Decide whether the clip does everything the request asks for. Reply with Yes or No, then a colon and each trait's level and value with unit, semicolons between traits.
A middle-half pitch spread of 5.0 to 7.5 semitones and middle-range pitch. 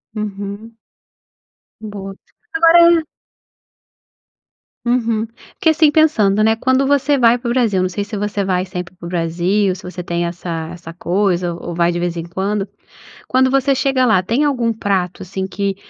No: wide, 5.4 semitones; high, 205 Hz